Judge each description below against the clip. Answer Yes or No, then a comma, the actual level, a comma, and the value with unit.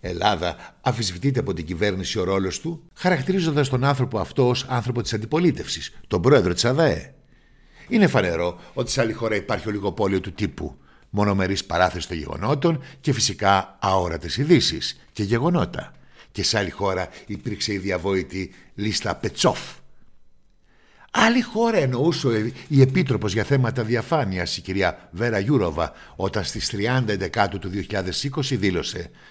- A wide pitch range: Yes, wide, 5.9 semitones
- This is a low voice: Yes, low, 105 Hz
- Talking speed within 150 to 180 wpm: No, average, 140 wpm